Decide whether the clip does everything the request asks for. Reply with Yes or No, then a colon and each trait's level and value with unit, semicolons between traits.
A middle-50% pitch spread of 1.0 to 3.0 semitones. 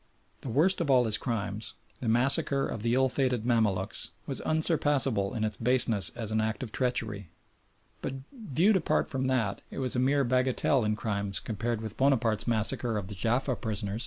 No: average, 3.5 semitones